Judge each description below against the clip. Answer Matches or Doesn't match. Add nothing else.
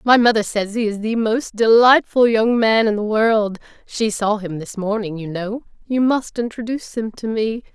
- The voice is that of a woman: Matches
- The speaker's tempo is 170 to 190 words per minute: Doesn't match